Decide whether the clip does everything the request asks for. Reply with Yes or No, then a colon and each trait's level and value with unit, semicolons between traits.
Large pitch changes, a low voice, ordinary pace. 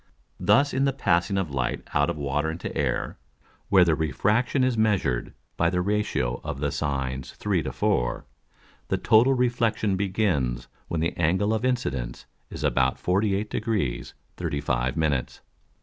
Yes: wide, 7.7 semitones; very low, 90 Hz; average, 150 wpm